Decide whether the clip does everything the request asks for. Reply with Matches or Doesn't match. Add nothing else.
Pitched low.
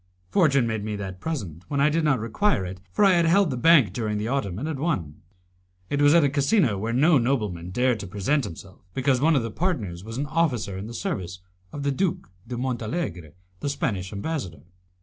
Matches